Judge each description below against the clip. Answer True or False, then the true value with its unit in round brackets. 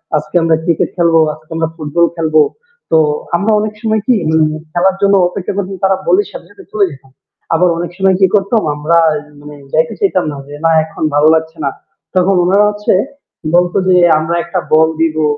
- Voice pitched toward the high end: False (170 Hz)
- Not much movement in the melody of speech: False (3.7 semitones)